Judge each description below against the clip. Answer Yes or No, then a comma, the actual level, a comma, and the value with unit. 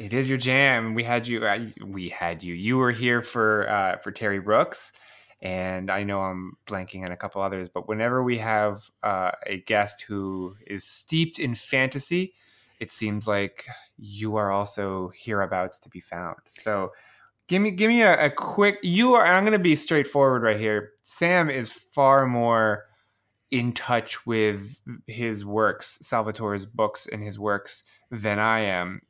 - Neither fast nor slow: Yes, average, 170 wpm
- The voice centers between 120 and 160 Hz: No, low, 110 Hz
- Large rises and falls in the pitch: No, average, 4.3 semitones